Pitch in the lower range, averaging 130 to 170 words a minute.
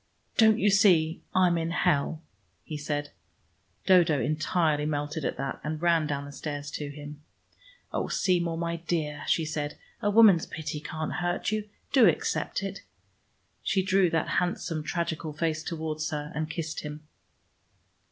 No: medium, 160 Hz; average, 150 wpm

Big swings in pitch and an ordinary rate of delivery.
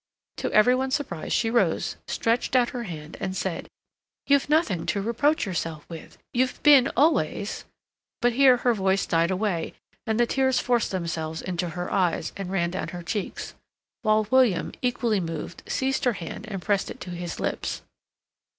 Yes: wide, 6.0 semitones; average, 170 wpm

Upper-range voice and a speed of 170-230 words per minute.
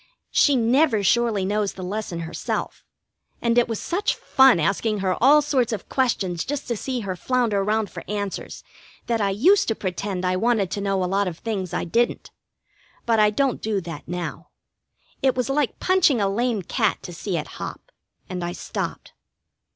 Yes: high, 215 Hz; average, 185 wpm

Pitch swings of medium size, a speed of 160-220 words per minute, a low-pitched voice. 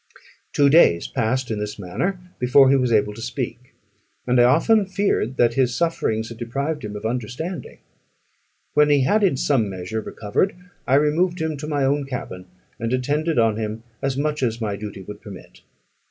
Yes: average, 5.0 semitones; average, 185 wpm; low, 125 Hz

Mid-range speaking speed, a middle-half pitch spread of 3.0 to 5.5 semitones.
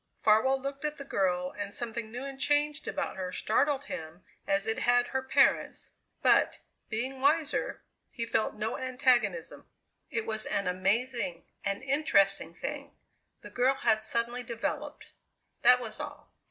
Yes: average, 150 wpm; average, 4.5 semitones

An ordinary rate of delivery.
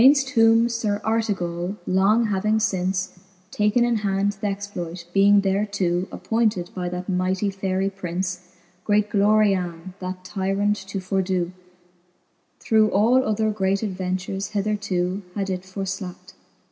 No: slow, 120 wpm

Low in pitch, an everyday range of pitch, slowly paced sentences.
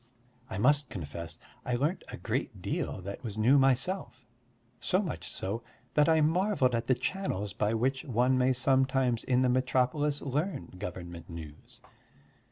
No: low, 130 Hz; average, 5.0 semitones; average, 155 wpm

